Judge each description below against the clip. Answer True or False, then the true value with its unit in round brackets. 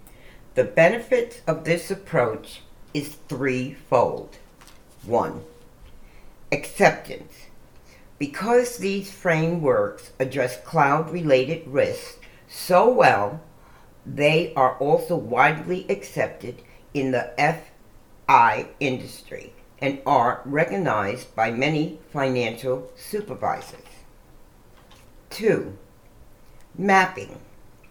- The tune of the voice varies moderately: False (6.6 semitones)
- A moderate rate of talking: False (75 wpm)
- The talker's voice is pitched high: False (150 Hz)